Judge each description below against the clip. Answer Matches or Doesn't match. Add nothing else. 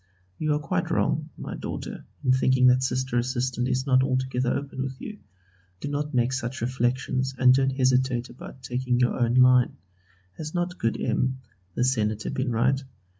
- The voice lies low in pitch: Matches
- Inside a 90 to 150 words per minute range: Doesn't match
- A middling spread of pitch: Doesn't match